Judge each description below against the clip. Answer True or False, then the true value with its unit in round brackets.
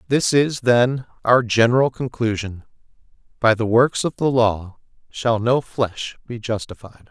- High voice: False (115 Hz)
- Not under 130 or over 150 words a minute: True (145 wpm)